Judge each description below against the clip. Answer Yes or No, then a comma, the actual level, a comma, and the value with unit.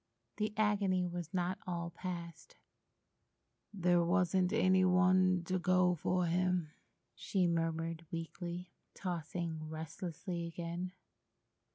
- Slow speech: Yes, slow, 100 wpm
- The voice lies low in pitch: No, medium, 175 Hz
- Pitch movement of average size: No, narrow, 1.6 semitones